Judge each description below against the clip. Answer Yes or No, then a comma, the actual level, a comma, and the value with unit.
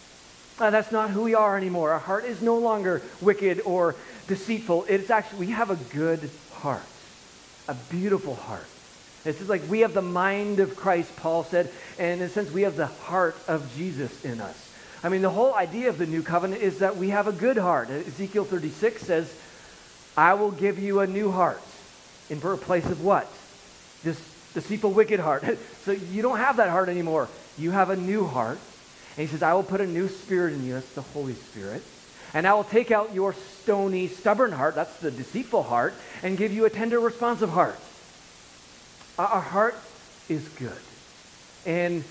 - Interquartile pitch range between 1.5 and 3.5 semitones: No, average, 4.7 semitones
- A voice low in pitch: No, medium, 180 Hz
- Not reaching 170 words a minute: No, average, 190 wpm